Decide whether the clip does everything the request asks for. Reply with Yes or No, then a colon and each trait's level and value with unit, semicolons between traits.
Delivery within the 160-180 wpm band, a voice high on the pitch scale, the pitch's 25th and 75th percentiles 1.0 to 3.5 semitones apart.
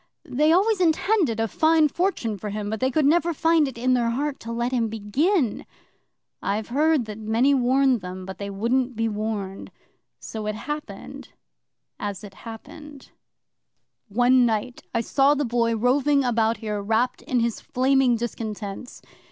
No: average, 165 wpm; high, 240 Hz; average, 4.4 semitones